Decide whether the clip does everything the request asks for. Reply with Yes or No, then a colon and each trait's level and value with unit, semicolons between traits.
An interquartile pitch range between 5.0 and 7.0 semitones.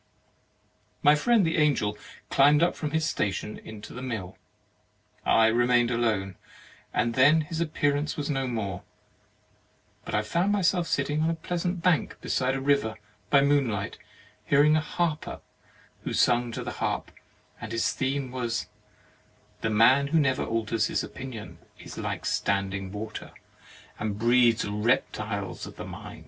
Yes: wide, 5.4 semitones